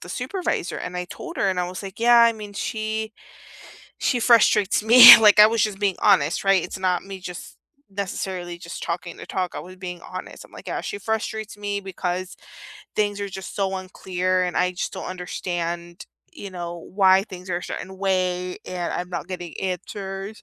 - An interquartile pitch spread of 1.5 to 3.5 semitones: Yes, narrow, 2.4 semitones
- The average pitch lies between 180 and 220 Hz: Yes, high, 190 Hz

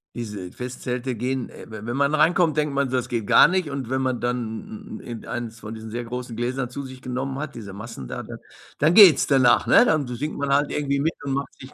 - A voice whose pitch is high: No, low, 130 Hz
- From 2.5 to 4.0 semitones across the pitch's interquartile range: Yes, average, 2.9 semitones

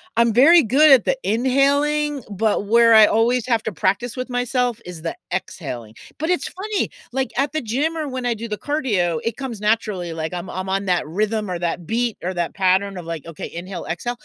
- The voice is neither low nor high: No, high, 225 Hz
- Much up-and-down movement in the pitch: Yes, wide, 5.9 semitones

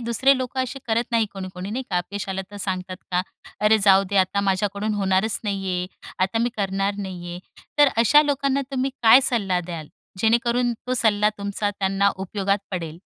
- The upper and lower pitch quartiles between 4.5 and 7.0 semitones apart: No, average, 3.5 semitones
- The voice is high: Yes, high, 200 Hz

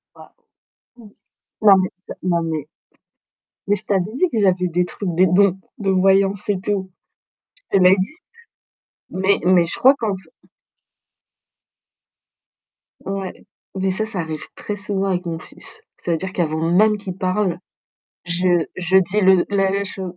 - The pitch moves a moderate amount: No, narrow, 2.0 semitones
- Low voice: No, high, 190 Hz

